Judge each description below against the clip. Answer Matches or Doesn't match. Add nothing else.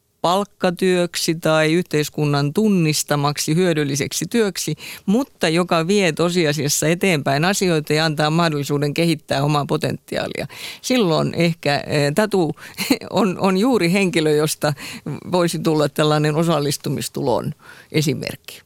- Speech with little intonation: Doesn't match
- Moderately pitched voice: Matches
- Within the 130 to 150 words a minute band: Doesn't match